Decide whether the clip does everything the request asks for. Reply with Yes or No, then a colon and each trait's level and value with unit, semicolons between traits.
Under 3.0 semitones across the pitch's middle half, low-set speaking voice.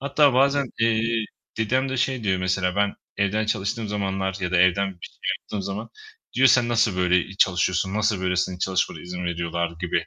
No: average, 3.9 semitones; low, 100 Hz